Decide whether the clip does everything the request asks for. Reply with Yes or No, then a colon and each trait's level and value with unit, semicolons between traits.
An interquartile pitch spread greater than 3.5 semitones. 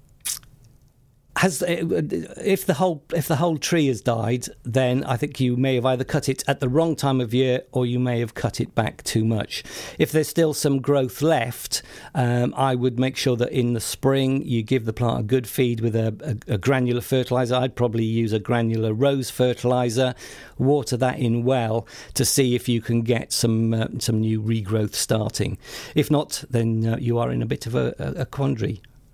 No: narrow, 2.6 semitones